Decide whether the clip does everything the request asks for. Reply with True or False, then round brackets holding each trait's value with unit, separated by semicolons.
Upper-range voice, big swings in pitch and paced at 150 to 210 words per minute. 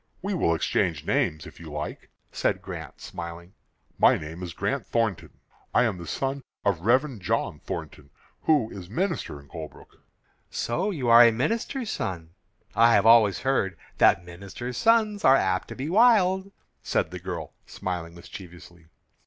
False (110 Hz; 8.3 semitones; 160 wpm)